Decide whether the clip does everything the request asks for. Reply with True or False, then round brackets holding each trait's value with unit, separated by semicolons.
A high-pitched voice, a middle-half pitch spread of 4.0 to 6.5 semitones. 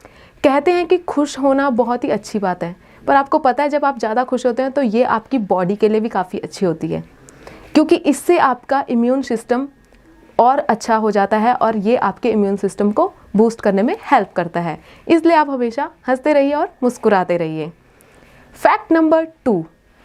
True (245 Hz; 5.6 semitones)